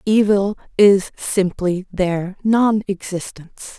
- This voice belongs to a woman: Yes, female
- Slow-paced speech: Yes, slow, 80 wpm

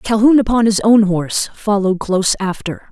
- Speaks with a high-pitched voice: Yes, high, 205 Hz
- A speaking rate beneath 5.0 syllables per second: No, 5.3 syllables/s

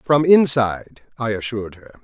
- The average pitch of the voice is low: Yes, low, 120 Hz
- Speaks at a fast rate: No, average, 145 wpm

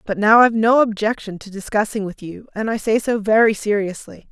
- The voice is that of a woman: Yes, female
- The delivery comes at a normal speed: No, fast, 210 wpm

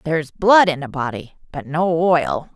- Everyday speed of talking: Yes, average, 190 wpm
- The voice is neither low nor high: Yes, medium, 160 Hz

